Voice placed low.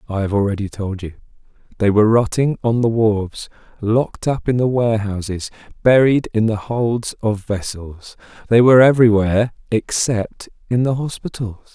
Yes: low, 110 Hz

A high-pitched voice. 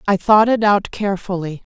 Yes: high, 195 Hz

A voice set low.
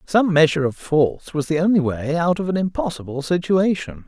No: medium, 160 Hz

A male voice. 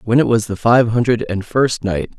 Yes: male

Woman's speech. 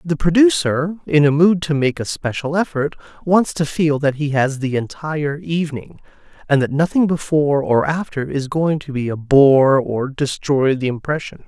No: male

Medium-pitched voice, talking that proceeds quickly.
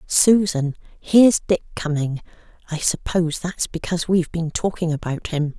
No: medium, 170 Hz; average, 140 wpm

